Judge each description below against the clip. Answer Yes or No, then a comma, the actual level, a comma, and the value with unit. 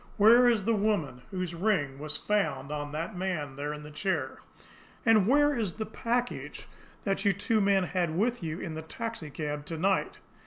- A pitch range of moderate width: No, wide, 6.0 semitones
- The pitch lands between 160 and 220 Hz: Yes, medium, 185 Hz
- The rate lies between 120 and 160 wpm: No, average, 185 wpm